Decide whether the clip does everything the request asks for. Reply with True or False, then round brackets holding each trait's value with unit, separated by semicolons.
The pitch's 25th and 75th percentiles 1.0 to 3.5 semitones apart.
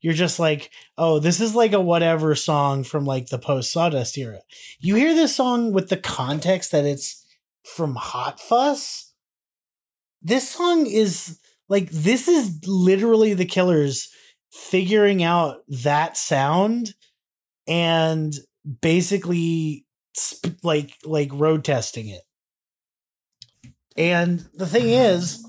False (5.4 semitones)